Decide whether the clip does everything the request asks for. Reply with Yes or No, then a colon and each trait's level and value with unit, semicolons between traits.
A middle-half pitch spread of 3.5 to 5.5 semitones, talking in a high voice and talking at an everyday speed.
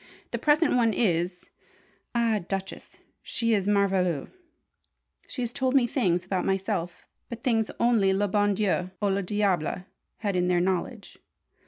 Yes: average, 4.0 semitones; high, 200 Hz; average, 150 wpm